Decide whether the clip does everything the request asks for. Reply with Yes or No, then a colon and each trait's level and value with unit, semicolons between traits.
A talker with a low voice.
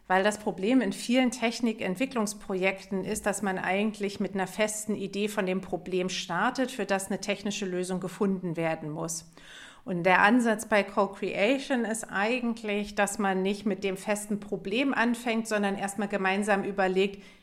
No: high, 200 Hz